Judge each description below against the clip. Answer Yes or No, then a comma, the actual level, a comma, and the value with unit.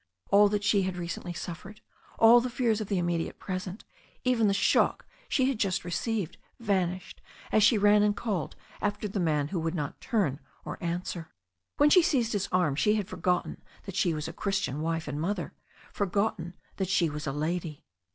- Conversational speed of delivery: Yes, average, 190 wpm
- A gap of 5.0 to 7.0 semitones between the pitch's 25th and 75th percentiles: No, average, 3.6 semitones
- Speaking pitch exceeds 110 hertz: Yes, high, 190 Hz